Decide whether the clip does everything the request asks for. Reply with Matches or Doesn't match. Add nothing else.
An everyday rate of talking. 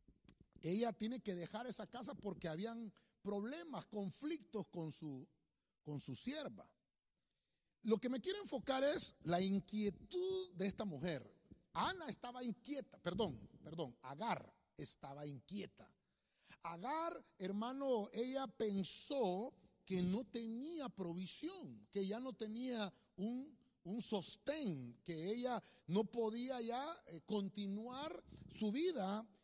Doesn't match